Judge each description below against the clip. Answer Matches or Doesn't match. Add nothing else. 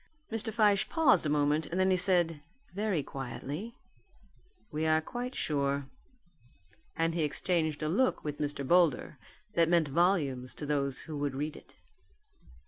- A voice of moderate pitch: Matches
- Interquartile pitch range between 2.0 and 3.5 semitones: Doesn't match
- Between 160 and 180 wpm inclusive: Doesn't match